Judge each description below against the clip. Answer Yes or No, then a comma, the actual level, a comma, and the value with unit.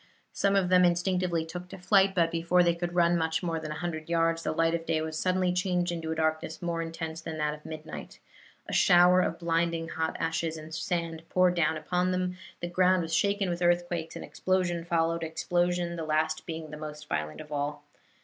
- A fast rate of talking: Yes, fast, 210 wpm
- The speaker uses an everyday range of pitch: No, narrow, 1.8 semitones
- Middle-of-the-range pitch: Yes, medium, 170 Hz